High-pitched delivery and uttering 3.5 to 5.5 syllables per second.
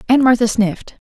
No: high, 230 Hz; 6.0 syllables/s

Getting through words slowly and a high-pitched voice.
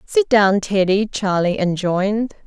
Yes: slow, 120 wpm; high, 200 Hz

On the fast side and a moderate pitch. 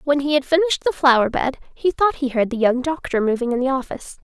No: fast, 250 wpm; very high, 275 Hz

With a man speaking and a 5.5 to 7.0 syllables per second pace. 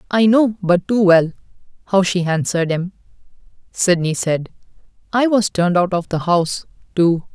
No: male; 5.0 syllables/s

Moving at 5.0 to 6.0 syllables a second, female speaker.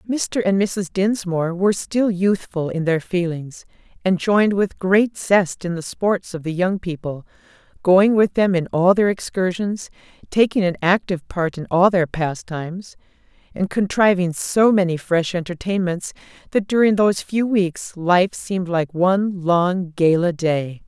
No: 4.4 syllables/s; female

